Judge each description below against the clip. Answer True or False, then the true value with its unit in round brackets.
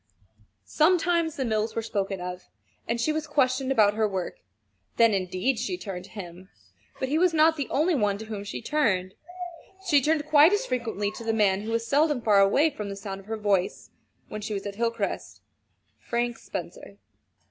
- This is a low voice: False (225 Hz)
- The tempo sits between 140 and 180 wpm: False (190 wpm)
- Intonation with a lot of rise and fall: True (6.4 semitones)